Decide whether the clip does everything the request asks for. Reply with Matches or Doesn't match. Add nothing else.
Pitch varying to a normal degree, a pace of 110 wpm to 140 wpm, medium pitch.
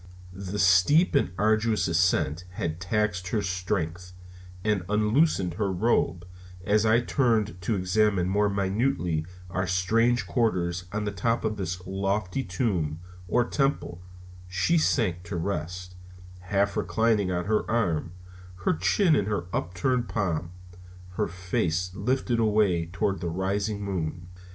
Doesn't match